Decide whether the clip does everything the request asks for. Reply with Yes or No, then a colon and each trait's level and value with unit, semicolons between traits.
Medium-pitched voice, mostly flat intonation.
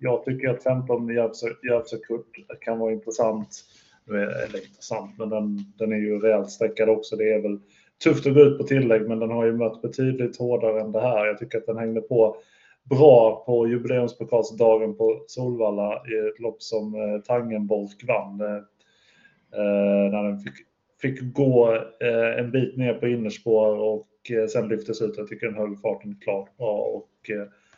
No: low, 110 Hz; narrow, 2.1 semitones